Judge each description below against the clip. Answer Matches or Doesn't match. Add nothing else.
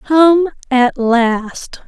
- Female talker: Matches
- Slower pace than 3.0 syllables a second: Matches